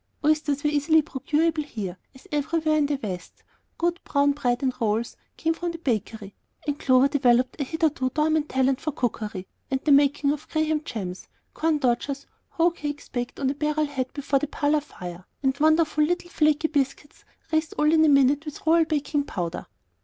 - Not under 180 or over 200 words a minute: Yes, average, 185 wpm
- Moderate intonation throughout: Yes, average, 3.2 semitones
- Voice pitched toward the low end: No, very high, 290 Hz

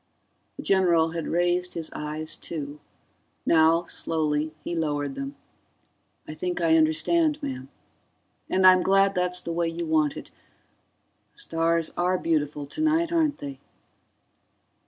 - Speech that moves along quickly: No, slow, 135 wpm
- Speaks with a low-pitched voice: No, medium, 165 Hz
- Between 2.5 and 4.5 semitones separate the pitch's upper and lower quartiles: Yes, average, 2.9 semitones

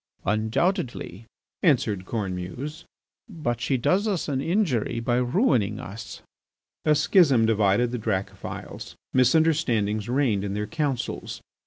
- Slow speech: Yes, slow, 115 wpm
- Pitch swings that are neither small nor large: No, wide, 6.2 semitones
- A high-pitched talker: No, low, 120 Hz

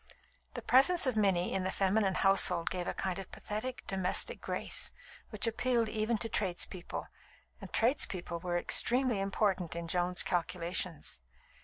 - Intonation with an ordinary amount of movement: Yes, average, 3.9 semitones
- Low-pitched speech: No, high, 195 Hz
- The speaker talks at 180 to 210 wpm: No, average, 145 wpm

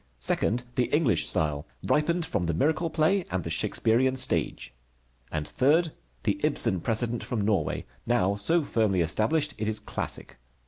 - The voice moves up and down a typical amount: No, wide, 8.1 semitones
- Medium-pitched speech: No, low, 115 Hz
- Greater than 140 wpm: Yes, average, 150 wpm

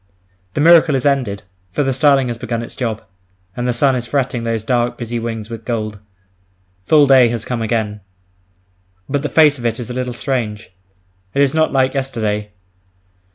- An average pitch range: Yes, average, 3.0 semitones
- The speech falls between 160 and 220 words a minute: Yes, average, 185 wpm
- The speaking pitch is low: Yes, low, 120 Hz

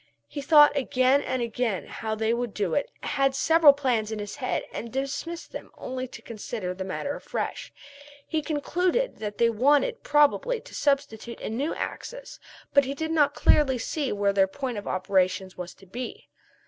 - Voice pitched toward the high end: Yes, very high, 255 Hz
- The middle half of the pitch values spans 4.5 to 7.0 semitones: Yes, average, 5.2 semitones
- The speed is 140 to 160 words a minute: No, average, 185 wpm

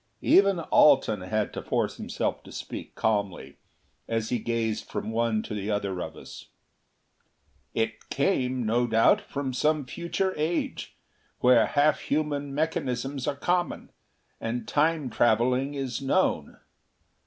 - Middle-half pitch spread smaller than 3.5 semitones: No, average, 4.6 semitones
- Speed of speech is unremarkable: No, slow, 130 wpm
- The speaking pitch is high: No, low, 125 Hz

